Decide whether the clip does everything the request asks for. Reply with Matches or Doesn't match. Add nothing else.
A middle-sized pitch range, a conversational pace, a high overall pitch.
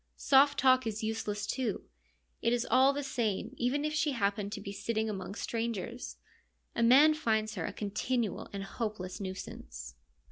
Matches